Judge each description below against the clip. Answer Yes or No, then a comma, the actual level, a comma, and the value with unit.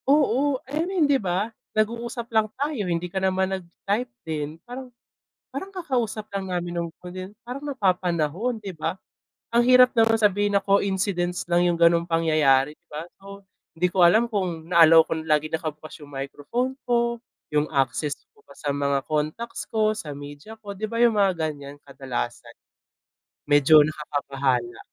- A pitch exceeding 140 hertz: Yes, medium, 185 Hz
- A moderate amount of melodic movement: No, wide, 6.6 semitones